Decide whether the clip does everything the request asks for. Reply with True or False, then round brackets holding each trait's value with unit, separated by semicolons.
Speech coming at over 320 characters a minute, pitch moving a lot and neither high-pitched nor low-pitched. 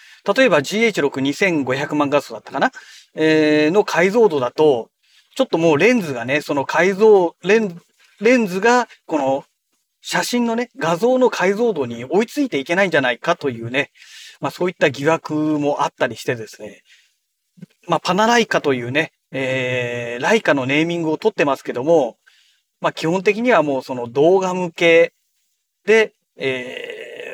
False (310 characters per minute; 7.4 semitones; 170 Hz)